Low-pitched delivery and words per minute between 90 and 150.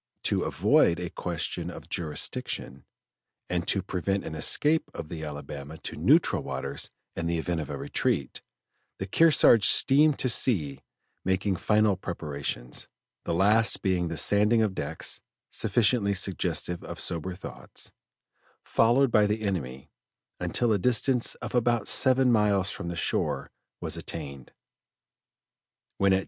Yes: very low, 95 Hz; average, 140 wpm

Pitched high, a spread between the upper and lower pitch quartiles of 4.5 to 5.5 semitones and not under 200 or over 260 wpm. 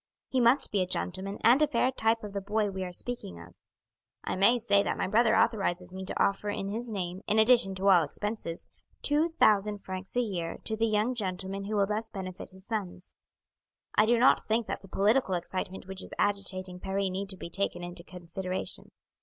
No: high, 200 Hz; average, 2.9 semitones; fast, 205 wpm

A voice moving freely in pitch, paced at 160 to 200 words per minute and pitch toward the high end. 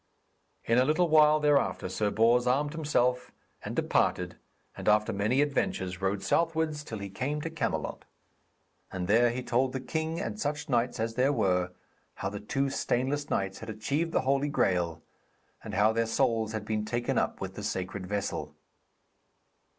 No: wide, 6.0 semitones; average, 170 wpm; low, 120 Hz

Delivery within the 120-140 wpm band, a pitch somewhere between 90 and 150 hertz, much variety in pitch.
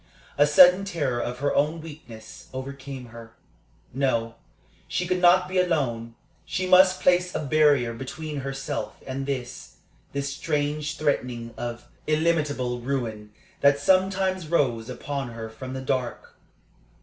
No: slow, 135 wpm; medium, 140 Hz; average, 4.7 semitones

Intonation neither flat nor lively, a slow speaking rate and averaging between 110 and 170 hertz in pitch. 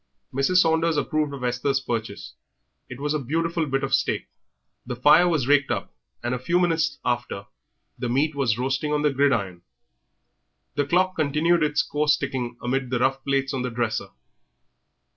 No: average, 3.4 semitones; average, 170 wpm; medium, 140 Hz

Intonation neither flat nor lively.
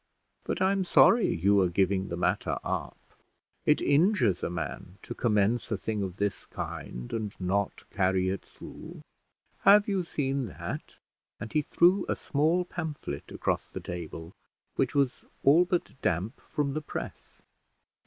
No: wide, 8.8 semitones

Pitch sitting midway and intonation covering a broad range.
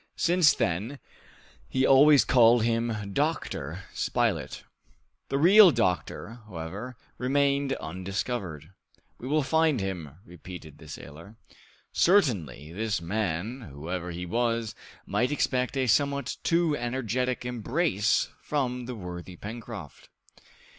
No: low, 115 Hz; wide, 7.0 semitones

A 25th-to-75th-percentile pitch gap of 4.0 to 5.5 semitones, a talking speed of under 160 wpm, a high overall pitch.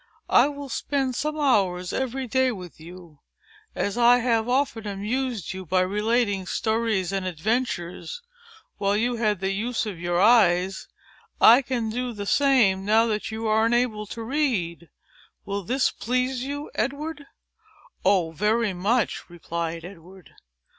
Yes: average, 4.9 semitones; average, 150 wpm; high, 220 Hz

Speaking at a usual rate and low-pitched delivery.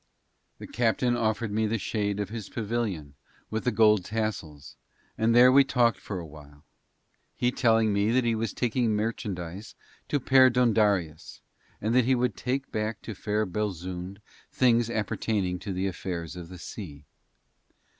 Yes: average, 155 wpm; low, 110 Hz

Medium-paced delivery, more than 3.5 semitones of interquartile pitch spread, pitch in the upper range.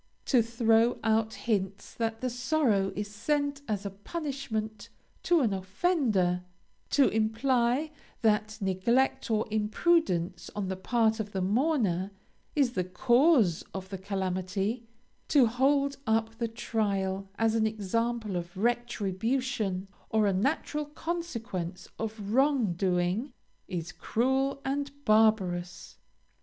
No: slow, 125 wpm; average, 4.9 semitones; high, 220 Hz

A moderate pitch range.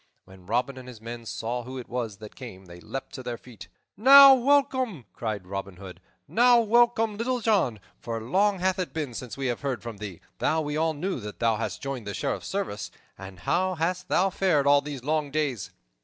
No: wide, 8.8 semitones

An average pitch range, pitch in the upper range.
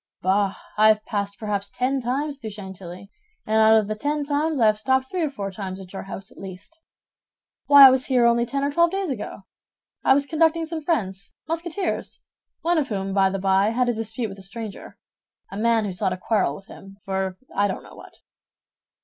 No: wide, 6.2 semitones; high, 220 Hz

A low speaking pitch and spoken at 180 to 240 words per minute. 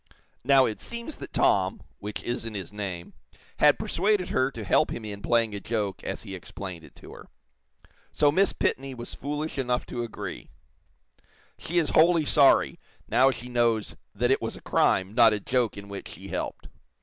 Yes: low, 120 Hz; average, 185 wpm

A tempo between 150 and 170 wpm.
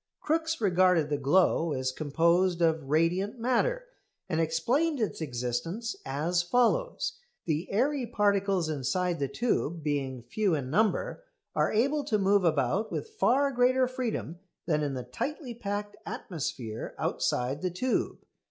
No: average, 140 wpm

